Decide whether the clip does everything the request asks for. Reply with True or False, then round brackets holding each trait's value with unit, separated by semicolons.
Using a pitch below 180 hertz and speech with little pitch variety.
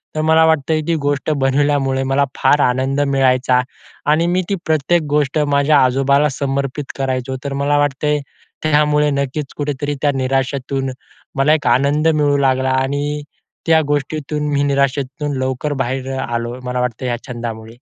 True (140 Hz; 1.9 semitones)